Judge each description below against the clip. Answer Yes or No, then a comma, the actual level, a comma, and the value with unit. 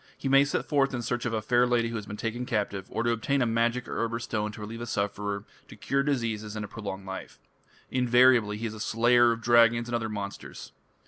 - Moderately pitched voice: No, low, 115 Hz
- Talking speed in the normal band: No, fast, 240 wpm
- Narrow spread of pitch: Yes, narrow, 2.3 semitones